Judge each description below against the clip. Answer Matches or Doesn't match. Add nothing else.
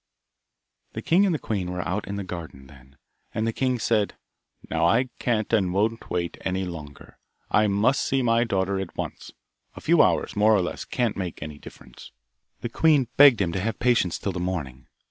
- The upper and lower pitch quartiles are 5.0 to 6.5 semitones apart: Doesn't match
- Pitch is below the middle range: Matches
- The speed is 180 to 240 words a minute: Matches